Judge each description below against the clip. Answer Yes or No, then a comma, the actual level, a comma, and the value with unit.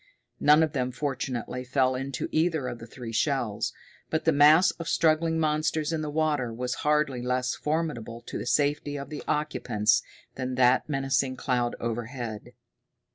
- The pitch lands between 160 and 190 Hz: No, low, 135 Hz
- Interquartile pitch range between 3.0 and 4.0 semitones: Yes, average, 3.5 semitones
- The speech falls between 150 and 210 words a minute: Yes, average, 160 wpm